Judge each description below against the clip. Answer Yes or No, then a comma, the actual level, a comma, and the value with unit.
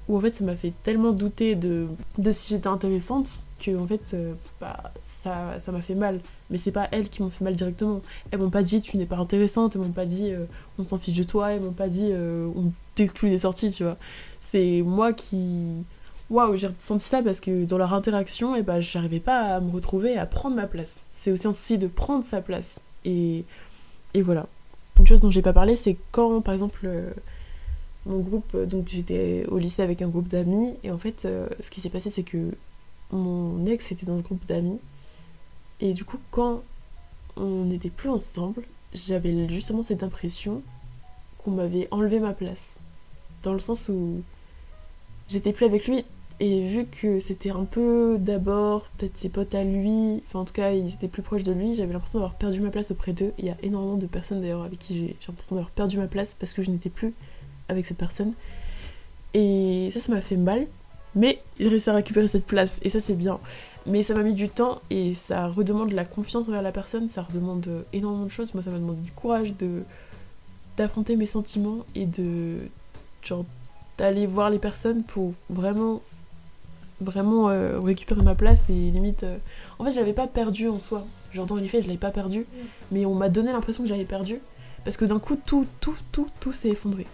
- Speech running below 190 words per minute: No, average, 215 wpm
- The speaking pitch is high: Yes, high, 195 Hz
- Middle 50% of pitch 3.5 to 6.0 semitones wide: No, average, 3.1 semitones